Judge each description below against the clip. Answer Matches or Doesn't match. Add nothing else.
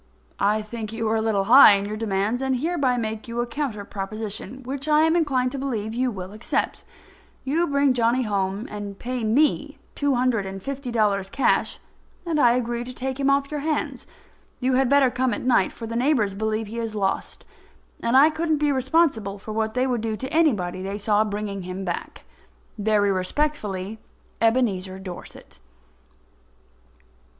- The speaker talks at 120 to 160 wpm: Doesn't match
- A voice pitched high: Matches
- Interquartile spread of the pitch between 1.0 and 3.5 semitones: Doesn't match